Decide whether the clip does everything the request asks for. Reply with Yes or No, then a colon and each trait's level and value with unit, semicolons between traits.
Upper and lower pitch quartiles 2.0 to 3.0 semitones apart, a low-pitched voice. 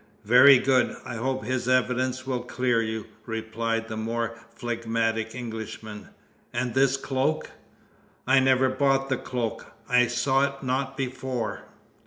Yes: narrow, 2.4 semitones; low, 125 Hz